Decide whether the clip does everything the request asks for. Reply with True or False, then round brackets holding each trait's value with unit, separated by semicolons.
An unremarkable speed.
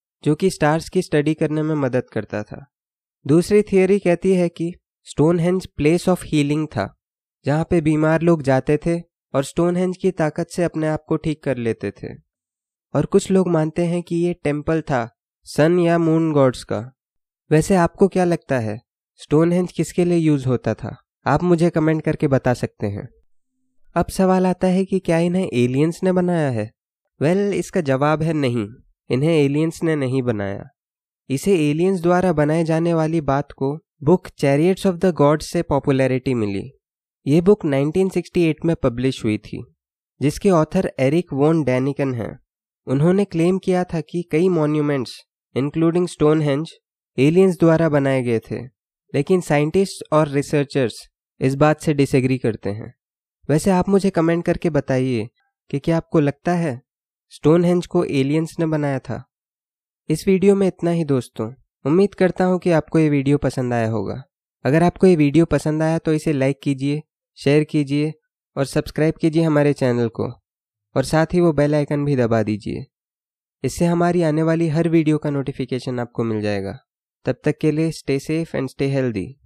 True (170 wpm)